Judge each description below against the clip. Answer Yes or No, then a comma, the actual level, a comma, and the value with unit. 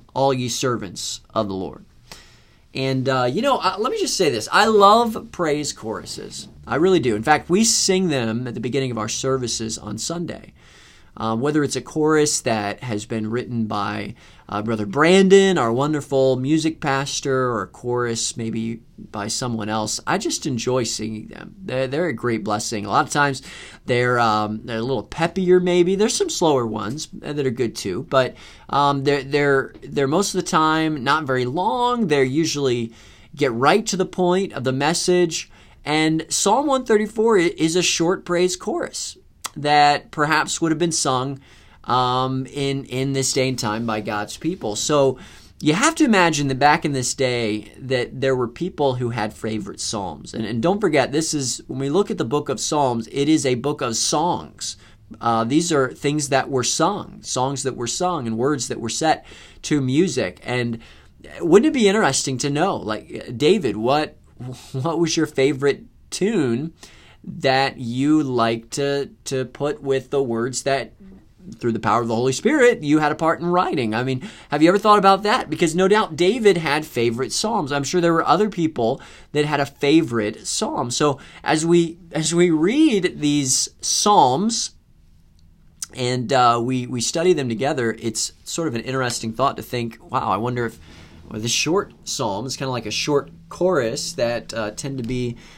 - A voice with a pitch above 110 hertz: Yes, low, 135 Hz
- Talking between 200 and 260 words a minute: No, average, 185 wpm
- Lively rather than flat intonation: Yes, wide, 5.8 semitones